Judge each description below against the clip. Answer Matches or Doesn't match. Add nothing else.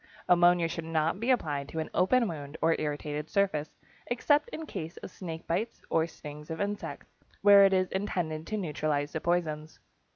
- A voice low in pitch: Doesn't match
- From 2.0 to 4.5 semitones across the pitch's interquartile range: Matches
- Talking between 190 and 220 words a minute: Doesn't match